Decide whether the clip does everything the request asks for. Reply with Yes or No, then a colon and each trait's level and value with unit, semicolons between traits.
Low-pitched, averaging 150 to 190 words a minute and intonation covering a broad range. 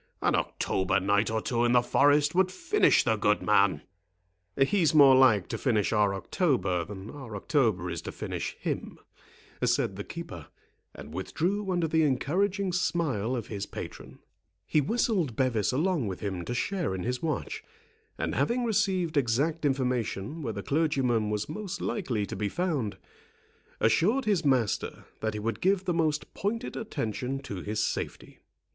Yes: low, 130 Hz; average, 165 wpm; wide, 8.4 semitones